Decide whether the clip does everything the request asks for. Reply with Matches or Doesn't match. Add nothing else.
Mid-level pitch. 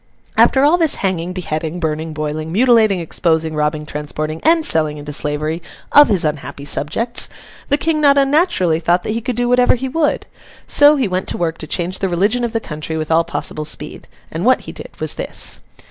Matches